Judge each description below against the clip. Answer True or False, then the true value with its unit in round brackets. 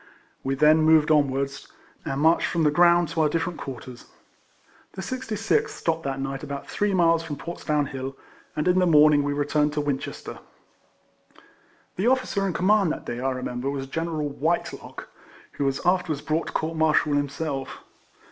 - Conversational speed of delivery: True (175 wpm)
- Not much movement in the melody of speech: False (3.5 semitones)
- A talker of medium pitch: True (155 Hz)